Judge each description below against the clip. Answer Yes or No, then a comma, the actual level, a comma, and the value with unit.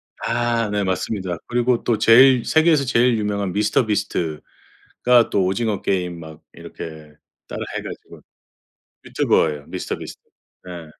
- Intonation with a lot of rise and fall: No, average, 5.0 semitones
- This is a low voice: Yes, low, 105 Hz